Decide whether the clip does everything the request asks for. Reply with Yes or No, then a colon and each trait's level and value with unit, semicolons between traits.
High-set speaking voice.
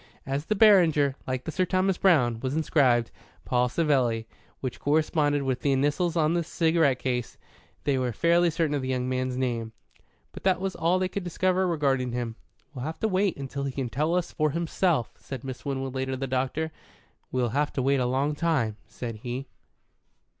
No: medium, 140 Hz